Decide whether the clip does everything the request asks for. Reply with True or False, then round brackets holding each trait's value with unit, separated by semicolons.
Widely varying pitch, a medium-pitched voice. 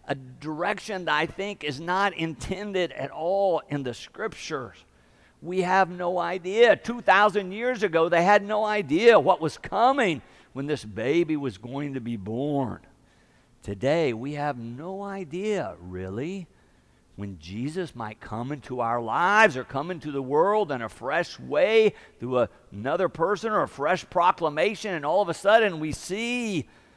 True (7.6 semitones; 165 Hz)